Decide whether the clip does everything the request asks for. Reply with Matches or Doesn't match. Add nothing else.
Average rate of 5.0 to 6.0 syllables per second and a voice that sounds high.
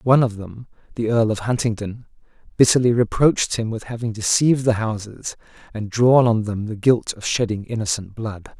Doesn't match